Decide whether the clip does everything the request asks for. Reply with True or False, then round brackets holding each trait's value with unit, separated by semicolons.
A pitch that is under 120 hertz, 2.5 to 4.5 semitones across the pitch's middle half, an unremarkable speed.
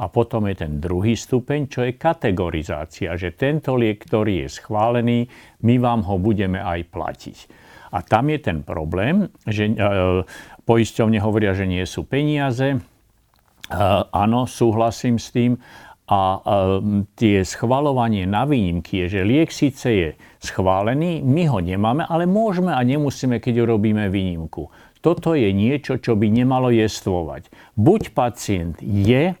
False (110 Hz; 4.9 semitones; 145 wpm)